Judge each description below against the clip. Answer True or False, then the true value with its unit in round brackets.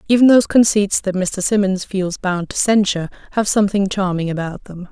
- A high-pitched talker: True (195 Hz)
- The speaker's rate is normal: True (185 wpm)